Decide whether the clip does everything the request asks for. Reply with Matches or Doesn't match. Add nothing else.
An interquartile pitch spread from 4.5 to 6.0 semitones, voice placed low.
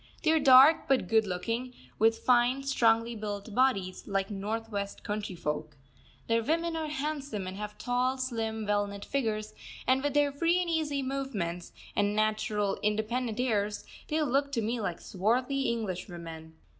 Doesn't match